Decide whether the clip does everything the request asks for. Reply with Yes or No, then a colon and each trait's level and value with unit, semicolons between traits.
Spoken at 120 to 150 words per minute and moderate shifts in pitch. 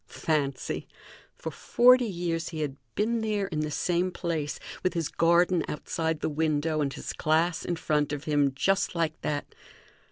No: average, 165 wpm; average, 3.0 semitones